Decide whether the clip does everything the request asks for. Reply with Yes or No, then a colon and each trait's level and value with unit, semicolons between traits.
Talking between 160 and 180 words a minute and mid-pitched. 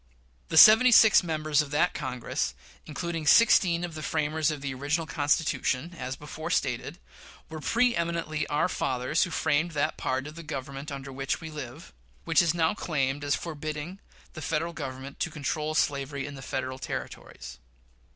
Yes: average, 170 wpm; medium, 150 Hz